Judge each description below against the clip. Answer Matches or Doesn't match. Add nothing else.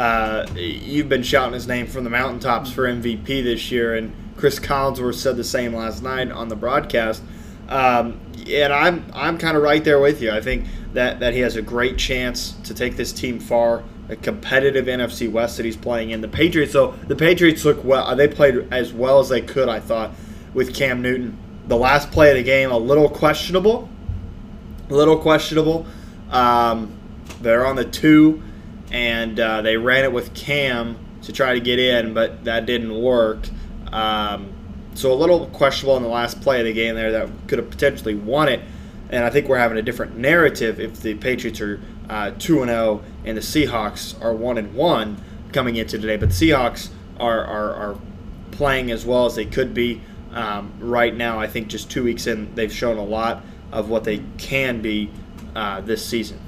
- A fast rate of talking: Doesn't match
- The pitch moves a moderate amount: Matches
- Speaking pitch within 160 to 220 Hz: Doesn't match